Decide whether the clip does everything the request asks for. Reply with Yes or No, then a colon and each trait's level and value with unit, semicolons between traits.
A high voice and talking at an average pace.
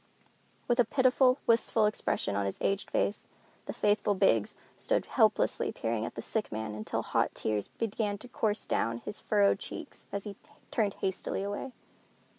Yes: high, 205 Hz; average, 165 wpm